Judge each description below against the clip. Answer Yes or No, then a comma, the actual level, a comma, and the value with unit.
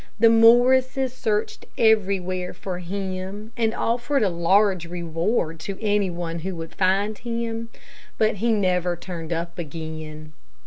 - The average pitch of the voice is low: No, high, 190 Hz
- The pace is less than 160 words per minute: Yes, slow, 135 wpm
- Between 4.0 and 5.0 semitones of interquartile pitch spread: Yes, average, 4.6 semitones